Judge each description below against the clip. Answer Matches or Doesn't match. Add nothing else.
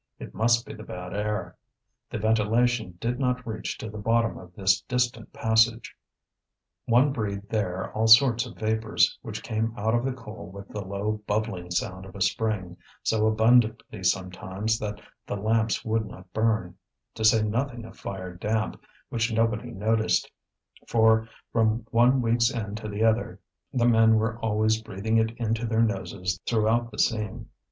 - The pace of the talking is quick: Doesn't match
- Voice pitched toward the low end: Matches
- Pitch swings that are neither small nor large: Doesn't match